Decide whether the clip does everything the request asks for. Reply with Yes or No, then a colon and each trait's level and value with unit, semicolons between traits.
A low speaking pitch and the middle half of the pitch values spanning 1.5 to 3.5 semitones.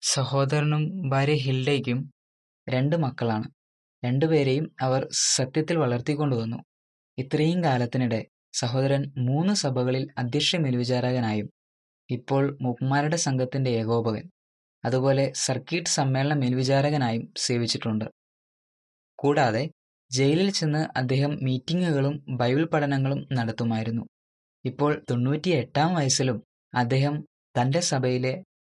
Yes: low, 130 Hz; average, 3.1 semitones